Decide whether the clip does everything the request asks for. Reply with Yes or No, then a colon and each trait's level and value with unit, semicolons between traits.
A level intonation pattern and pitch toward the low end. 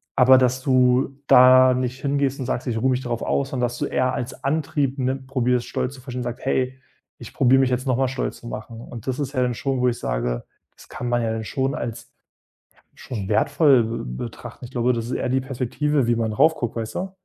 Yes: narrow, 1.9 semitones; low, 125 Hz